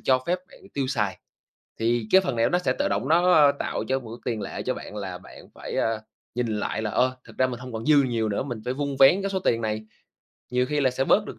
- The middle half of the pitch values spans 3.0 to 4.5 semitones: Yes, average, 4.0 semitones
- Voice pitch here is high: No, low, 125 Hz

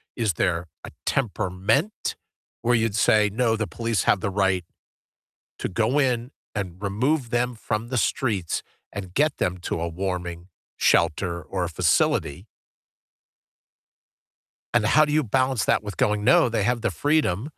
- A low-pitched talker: Yes, low, 105 Hz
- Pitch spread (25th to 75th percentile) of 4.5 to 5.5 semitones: Yes, average, 5.0 semitones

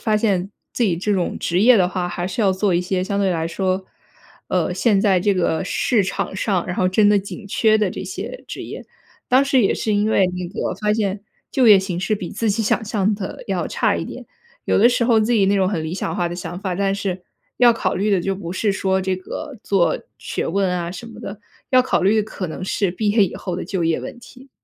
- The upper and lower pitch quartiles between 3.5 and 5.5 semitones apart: No, average, 2.8 semitones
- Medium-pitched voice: No, high, 195 Hz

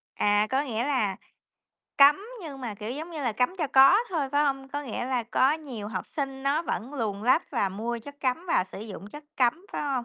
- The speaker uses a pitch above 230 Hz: Yes, very high, 265 Hz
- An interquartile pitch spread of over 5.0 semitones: No, average, 4.4 semitones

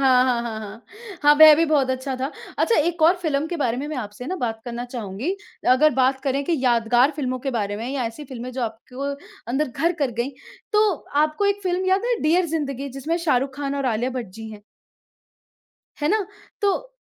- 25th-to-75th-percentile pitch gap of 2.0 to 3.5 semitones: No, average, 4.3 semitones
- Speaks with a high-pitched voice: Yes, very high, 275 Hz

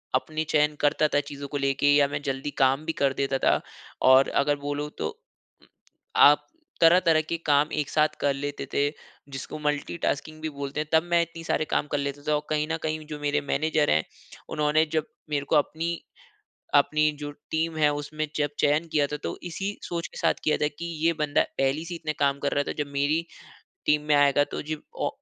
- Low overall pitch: No, medium, 150 Hz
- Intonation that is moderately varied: No, narrow, 1.6 semitones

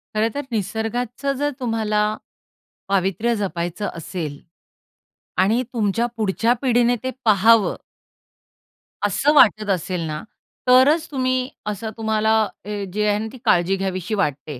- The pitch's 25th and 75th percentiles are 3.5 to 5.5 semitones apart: Yes, average, 3.8 semitones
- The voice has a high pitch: Yes, high, 215 Hz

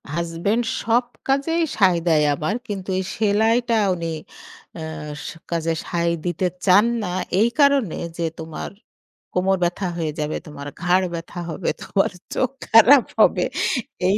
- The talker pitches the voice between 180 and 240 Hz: Yes, high, 190 Hz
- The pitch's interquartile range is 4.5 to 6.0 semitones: Yes, average, 5.1 semitones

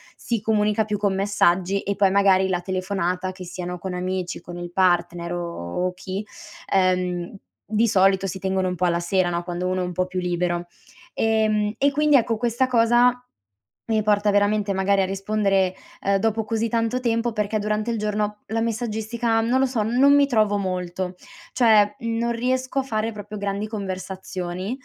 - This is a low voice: No, high, 200 Hz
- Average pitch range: Yes, average, 3.3 semitones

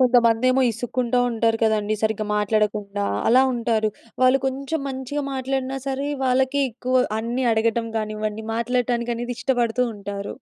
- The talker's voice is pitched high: Yes, high, 235 Hz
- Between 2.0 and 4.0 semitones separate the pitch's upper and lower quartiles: Yes, average, 2.8 semitones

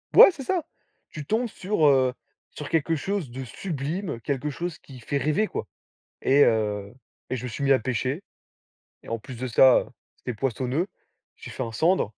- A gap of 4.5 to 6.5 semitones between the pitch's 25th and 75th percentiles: Yes, average, 5.0 semitones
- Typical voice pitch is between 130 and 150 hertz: Yes, medium, 140 Hz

